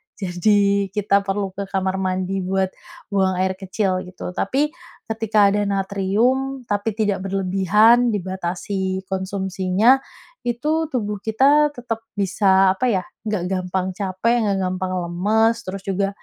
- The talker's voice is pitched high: Yes, high, 195 Hz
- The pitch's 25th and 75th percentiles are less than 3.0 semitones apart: Yes, narrow, 2.6 semitones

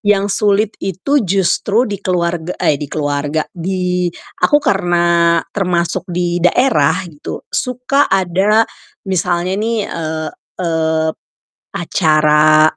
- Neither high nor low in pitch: Yes, medium, 180 Hz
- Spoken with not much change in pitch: No, average, 3.6 semitones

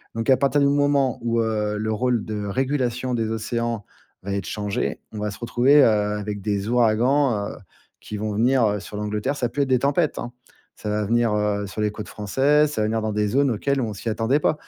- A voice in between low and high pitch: No, low, 115 Hz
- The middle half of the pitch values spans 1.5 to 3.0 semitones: No, average, 3.7 semitones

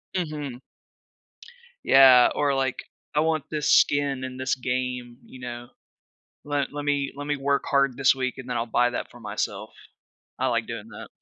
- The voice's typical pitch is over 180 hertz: No, low, 135 Hz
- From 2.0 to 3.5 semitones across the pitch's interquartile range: Yes, narrow, 2.4 semitones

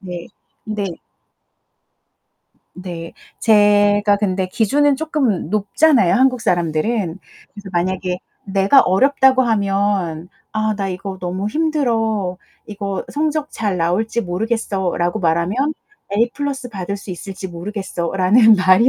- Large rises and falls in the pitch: No, average, 3.7 semitones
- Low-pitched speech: No, high, 200 Hz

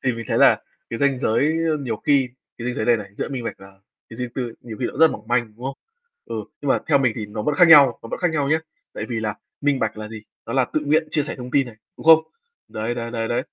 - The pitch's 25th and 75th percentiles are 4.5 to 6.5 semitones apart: No, average, 4.0 semitones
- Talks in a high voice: No, low, 125 Hz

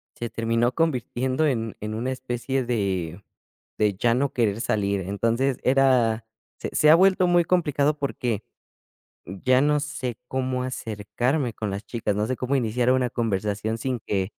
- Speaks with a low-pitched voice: Yes, low, 120 Hz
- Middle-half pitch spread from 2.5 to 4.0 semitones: Yes, average, 3.7 semitones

